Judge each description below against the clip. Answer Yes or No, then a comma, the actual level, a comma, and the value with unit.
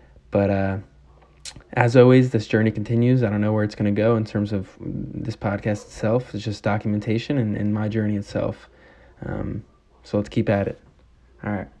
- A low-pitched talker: Yes, low, 105 Hz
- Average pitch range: No, narrow, 1.8 semitones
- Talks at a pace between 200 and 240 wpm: No, average, 190 wpm